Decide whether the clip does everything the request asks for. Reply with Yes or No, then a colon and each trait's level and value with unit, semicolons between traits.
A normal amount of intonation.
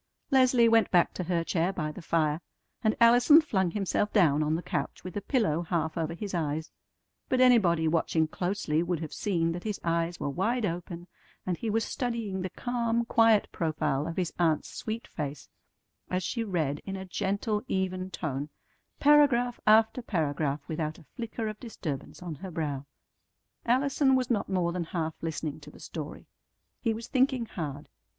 No: wide, 5.9 semitones